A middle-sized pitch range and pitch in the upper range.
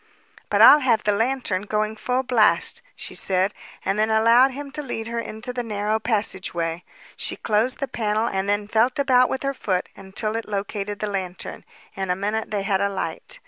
Yes: average, 3.5 semitones; high, 215 Hz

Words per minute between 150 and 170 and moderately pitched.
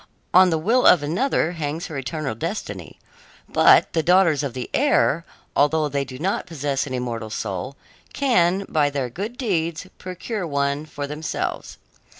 Yes: average, 155 wpm; medium, 155 Hz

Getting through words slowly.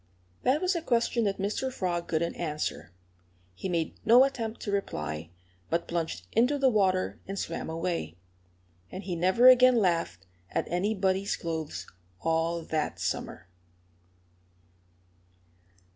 Yes: slow, 130 wpm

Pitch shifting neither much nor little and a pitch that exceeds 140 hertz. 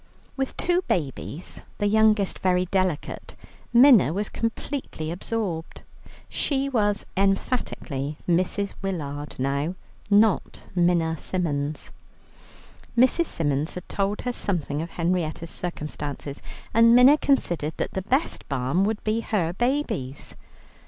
No: wide, 6.1 semitones; medium, 185 Hz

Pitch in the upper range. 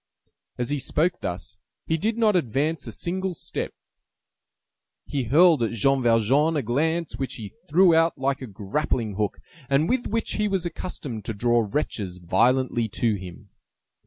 No: low, 135 Hz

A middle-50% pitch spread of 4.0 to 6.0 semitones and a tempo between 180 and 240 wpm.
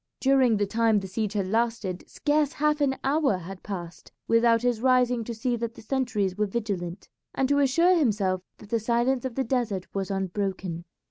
Yes: average, 4.9 semitones; average, 190 wpm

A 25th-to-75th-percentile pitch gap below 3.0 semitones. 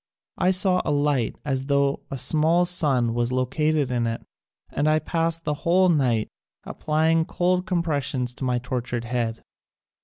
No: average, 4.7 semitones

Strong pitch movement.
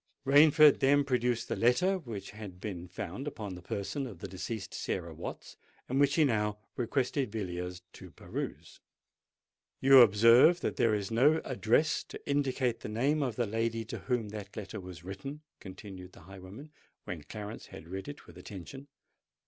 Yes: wide, 5.8 semitones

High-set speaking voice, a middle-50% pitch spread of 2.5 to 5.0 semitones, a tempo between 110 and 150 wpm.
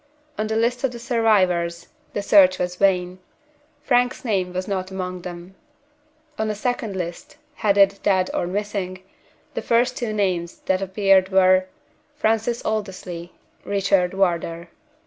Yes: high, 195 Hz; average, 2.9 semitones; average, 140 wpm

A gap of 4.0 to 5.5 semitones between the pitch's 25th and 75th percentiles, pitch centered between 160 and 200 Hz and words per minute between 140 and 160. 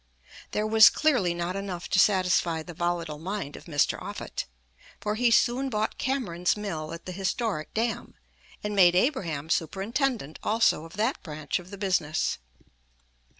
Yes: average, 4.4 semitones; high, 190 Hz; average, 150 wpm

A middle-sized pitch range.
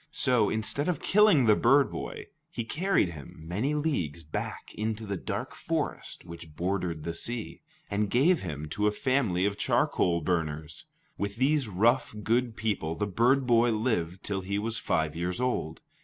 No: wide, 6.3 semitones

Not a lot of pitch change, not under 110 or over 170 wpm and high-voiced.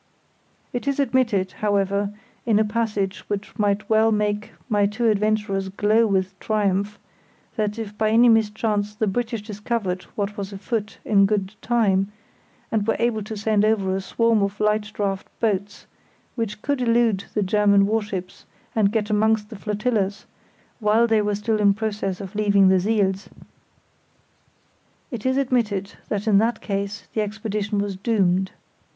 Yes: narrow, 1.8 semitones; average, 155 wpm; high, 210 Hz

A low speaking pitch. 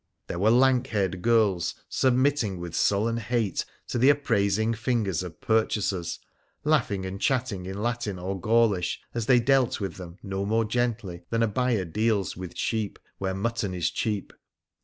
Yes: low, 110 Hz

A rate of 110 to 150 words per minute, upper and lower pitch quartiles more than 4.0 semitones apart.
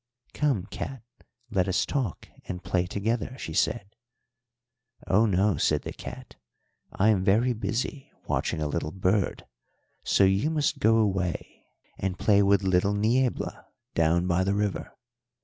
No: average, 145 wpm; average, 3.4 semitones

